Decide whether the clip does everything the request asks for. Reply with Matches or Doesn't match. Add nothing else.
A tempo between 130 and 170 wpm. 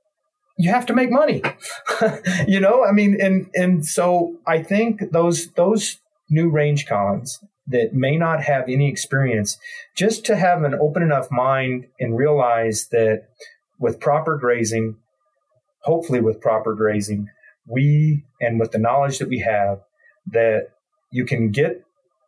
Matches